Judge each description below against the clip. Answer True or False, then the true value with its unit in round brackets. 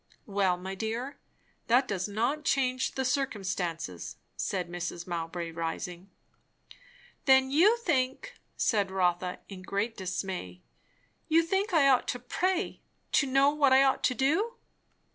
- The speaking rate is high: False (135 wpm)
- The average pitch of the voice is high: True (235 Hz)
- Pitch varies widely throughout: True (7.1 semitones)